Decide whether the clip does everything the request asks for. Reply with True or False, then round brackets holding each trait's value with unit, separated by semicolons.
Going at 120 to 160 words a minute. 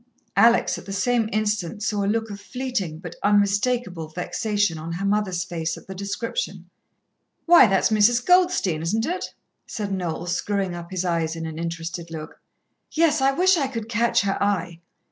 False (175 wpm)